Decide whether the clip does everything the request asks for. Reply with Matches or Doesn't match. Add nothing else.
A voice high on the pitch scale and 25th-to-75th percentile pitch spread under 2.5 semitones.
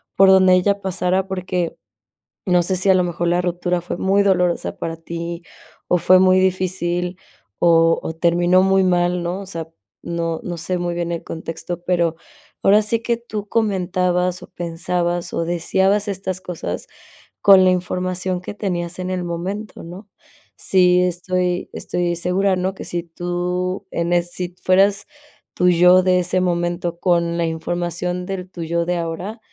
Doesn't match